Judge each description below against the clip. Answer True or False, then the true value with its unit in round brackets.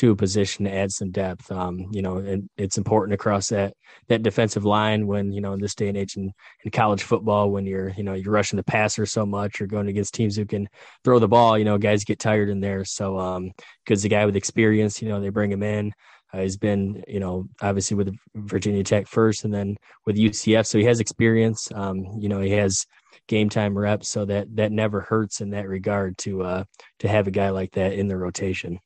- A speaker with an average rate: False (235 wpm)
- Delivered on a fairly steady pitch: True (1.5 semitones)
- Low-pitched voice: True (100 Hz)